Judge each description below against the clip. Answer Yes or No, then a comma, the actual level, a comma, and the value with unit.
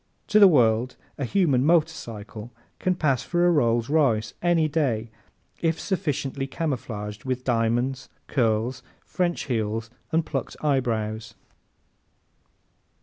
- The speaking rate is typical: No, slow, 115 wpm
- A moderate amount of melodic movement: No, wide, 5.8 semitones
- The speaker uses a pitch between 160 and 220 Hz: No, low, 130 Hz